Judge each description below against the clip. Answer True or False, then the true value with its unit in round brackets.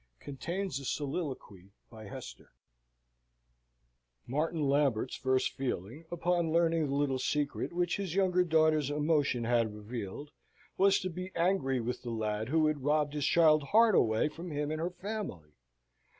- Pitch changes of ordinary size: True (4.9 semitones)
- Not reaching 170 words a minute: True (150 wpm)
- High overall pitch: False (150 Hz)